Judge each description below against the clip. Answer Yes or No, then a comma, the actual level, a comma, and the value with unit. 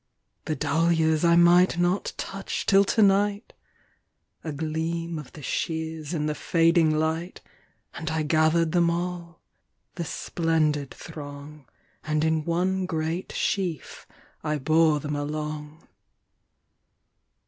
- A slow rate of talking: Yes, slow, 105 wpm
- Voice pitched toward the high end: No, medium, 160 Hz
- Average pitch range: No, narrow, 2.1 semitones